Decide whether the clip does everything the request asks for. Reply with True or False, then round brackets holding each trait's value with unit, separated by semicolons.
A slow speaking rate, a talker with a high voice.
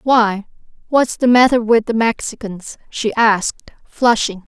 True (130 wpm; 225 Hz)